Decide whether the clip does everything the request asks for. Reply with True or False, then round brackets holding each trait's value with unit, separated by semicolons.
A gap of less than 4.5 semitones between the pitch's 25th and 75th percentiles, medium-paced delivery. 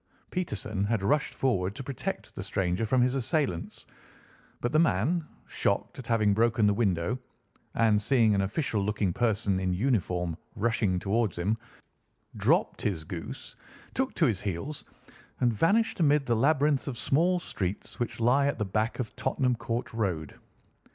False (5.1 semitones; 160 wpm)